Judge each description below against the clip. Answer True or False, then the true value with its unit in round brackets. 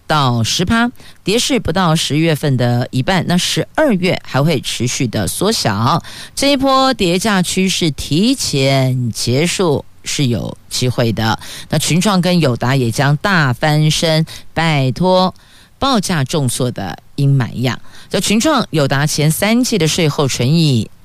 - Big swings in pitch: True (6.6 semitones)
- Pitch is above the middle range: False (155 Hz)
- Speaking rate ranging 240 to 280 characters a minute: False (210 characters per minute)